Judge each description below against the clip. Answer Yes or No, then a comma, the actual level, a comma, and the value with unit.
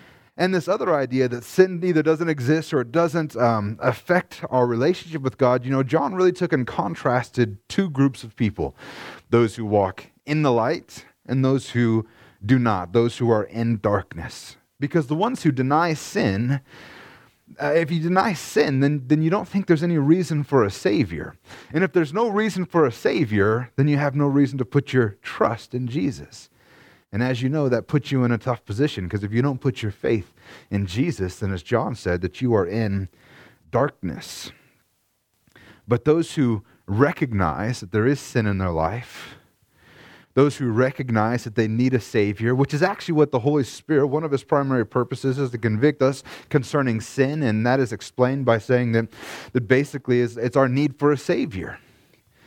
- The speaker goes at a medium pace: Yes, average, 190 wpm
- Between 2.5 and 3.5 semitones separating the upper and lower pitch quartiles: No, average, 4.5 semitones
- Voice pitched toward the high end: No, low, 130 Hz